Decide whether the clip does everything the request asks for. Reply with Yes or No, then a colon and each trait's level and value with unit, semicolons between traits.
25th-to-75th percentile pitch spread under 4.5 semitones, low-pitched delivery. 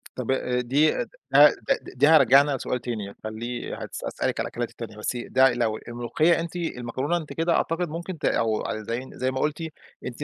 No: average, 4.8 semitones; low, 130 Hz